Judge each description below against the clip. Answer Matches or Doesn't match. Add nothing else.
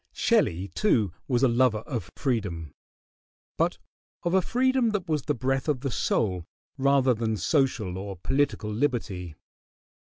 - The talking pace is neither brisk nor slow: Matches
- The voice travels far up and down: Matches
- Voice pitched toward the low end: Matches